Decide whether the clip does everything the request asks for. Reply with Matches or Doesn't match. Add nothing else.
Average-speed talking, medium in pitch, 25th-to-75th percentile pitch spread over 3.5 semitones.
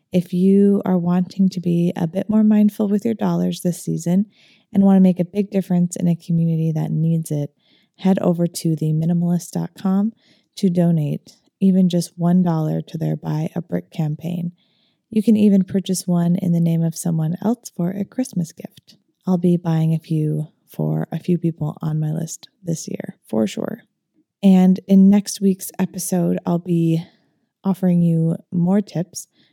Doesn't match